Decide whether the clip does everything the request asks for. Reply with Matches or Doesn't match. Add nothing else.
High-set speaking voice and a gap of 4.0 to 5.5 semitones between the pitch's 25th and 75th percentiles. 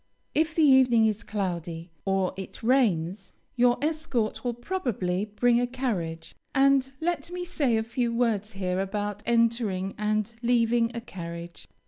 Matches